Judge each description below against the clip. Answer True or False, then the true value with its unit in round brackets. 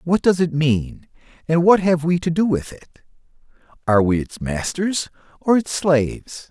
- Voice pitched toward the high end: False (160 Hz)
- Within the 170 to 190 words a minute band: True (175 wpm)